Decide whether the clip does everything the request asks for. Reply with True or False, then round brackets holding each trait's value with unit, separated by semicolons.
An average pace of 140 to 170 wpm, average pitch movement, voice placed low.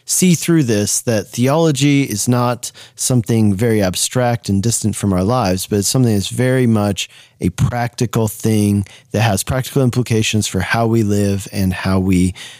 True (165 wpm; 3.7 semitones; 115 Hz)